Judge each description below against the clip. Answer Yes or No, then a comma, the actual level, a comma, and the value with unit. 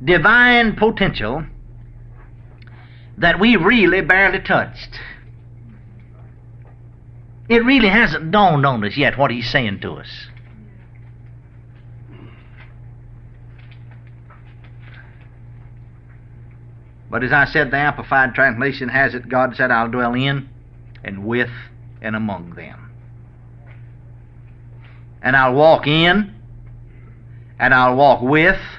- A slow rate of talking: Yes, slow, 95 wpm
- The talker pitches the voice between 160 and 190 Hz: No, low, 120 Hz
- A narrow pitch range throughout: Yes, narrow, 1.8 semitones